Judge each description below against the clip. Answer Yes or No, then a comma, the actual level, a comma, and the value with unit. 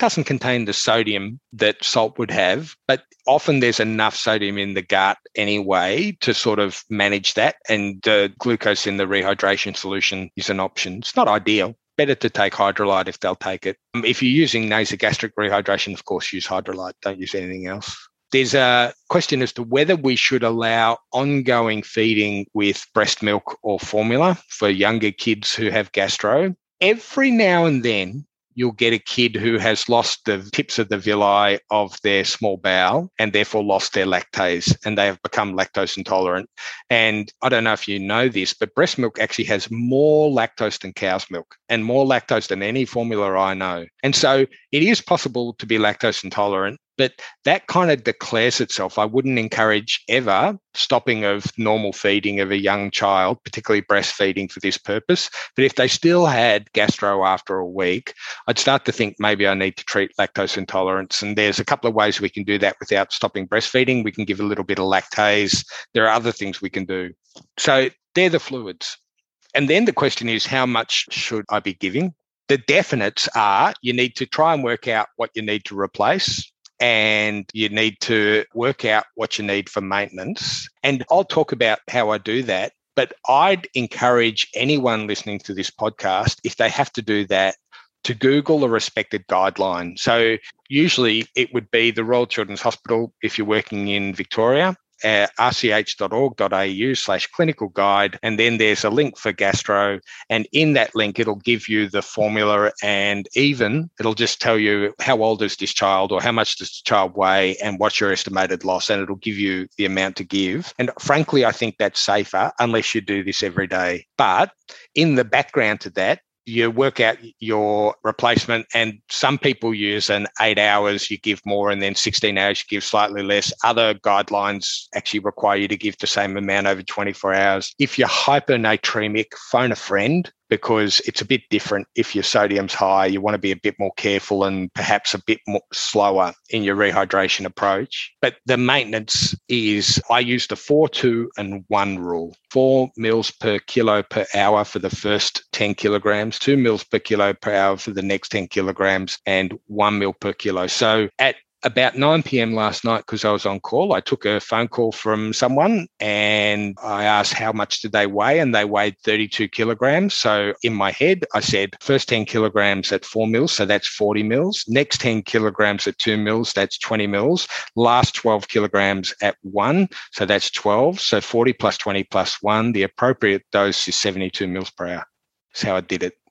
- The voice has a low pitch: Yes, low, 105 Hz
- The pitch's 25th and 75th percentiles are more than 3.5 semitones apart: No, average, 3.1 semitones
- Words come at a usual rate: Yes, average, 190 wpm